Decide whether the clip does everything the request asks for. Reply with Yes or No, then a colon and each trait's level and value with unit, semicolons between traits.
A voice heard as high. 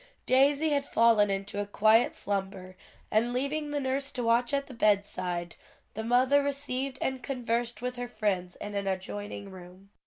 Yes: high, 230 Hz